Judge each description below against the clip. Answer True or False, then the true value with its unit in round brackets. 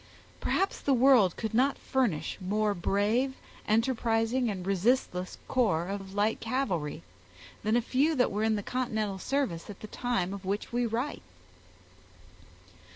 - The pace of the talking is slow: False (145 wpm)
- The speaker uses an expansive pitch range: False (4.3 semitones)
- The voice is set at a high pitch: True (220 Hz)